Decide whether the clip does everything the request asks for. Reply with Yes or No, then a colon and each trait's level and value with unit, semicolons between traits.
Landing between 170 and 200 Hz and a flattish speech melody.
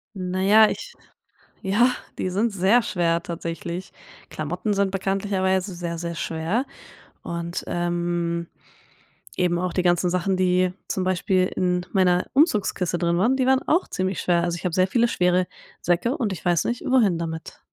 Yes: medium, 185 Hz; narrow, 2.3 semitones